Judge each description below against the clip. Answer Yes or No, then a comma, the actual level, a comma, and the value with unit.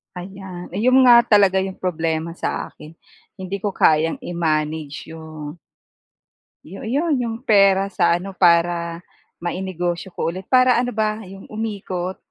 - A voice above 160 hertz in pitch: Yes, medium, 185 Hz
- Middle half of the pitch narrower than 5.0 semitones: Yes, average, 3.8 semitones